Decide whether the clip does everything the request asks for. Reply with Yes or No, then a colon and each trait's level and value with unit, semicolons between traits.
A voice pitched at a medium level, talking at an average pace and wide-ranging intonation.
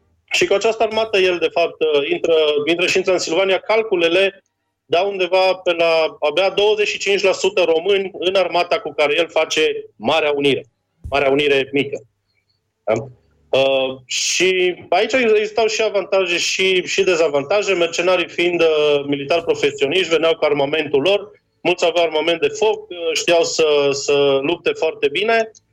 Yes: medium, 175 Hz; average, 140 wpm; wide, 6.2 semitones